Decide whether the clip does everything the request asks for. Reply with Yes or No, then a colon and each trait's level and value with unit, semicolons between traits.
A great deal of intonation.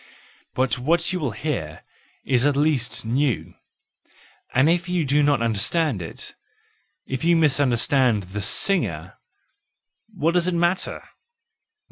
Yes: wide, 5.7 semitones